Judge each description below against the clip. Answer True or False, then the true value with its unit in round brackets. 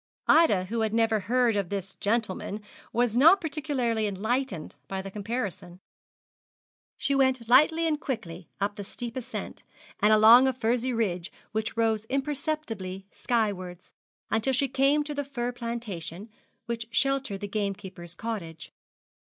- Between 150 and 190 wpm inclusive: False (140 wpm)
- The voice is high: True (225 Hz)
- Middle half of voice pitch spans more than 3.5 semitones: True (4.6 semitones)